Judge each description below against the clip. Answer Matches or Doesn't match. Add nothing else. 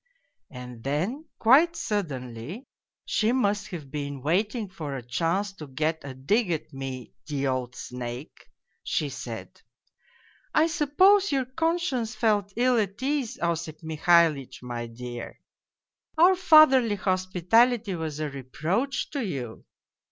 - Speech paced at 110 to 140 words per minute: Matches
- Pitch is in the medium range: Matches